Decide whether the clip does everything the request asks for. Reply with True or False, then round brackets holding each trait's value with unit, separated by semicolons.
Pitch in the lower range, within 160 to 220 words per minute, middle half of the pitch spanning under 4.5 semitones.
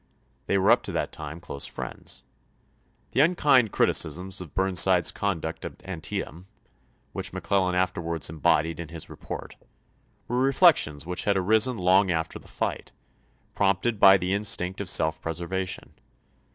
False (95 Hz; 150 wpm; 3.4 semitones)